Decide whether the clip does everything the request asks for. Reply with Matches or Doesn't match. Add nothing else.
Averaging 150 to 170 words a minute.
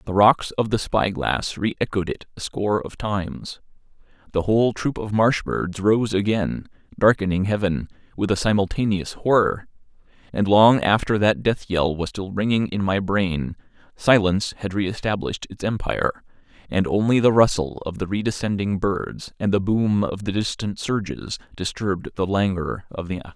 Matches